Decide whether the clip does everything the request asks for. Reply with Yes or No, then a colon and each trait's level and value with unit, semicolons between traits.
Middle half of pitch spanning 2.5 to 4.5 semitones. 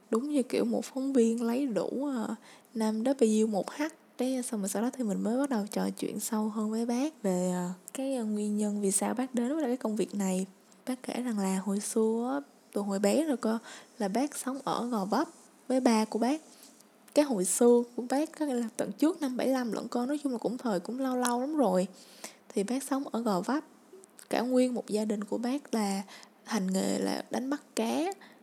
Yes: average, 3.8 semitones